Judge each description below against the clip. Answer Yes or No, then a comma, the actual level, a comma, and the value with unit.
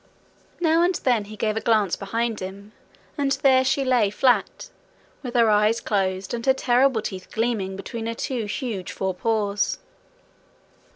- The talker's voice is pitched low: No, high, 225 Hz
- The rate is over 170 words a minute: No, average, 155 wpm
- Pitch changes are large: No, average, 3.8 semitones